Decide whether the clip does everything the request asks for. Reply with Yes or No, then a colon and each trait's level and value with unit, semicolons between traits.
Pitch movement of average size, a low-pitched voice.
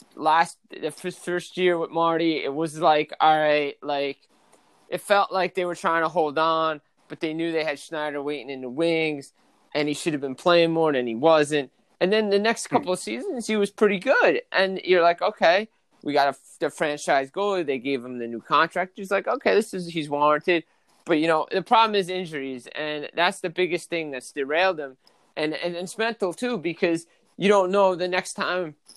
No: average, 3.7 semitones; medium, 165 Hz